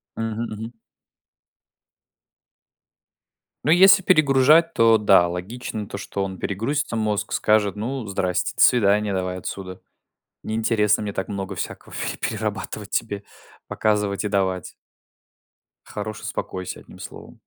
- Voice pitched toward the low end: Yes, low, 105 Hz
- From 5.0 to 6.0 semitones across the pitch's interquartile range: No, narrow, 2.5 semitones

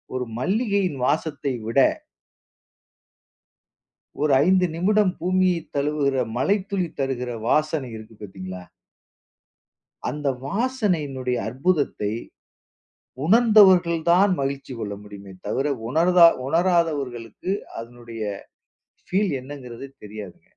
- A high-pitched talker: No, medium, 145 Hz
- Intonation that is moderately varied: No, wide, 6.7 semitones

